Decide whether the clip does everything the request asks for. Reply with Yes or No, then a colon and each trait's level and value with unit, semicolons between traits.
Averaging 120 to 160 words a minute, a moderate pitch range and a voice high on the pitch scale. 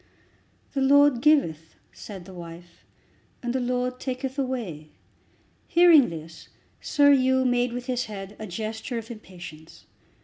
No: slow, 135 wpm; wide, 6.3 semitones; high, 245 Hz